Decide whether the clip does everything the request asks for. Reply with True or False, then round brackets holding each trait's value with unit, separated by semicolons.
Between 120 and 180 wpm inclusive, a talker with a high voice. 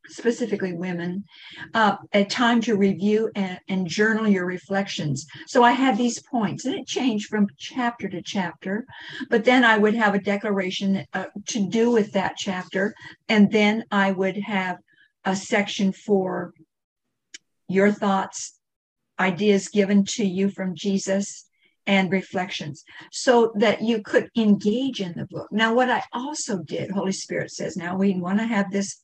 True (160 wpm; 200 Hz)